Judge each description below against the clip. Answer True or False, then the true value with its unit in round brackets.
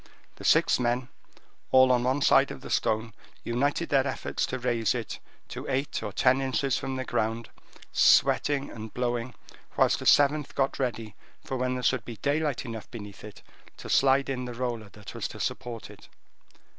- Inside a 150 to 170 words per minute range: False (180 wpm)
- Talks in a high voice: False (125 Hz)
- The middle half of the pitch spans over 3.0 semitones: False (2.5 semitones)